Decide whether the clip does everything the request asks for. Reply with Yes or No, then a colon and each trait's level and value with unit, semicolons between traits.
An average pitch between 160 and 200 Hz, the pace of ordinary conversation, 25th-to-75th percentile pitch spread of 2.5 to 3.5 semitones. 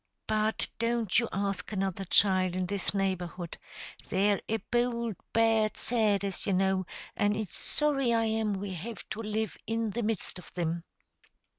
No: high, 210 Hz; average, 160 wpm; average, 2.9 semitones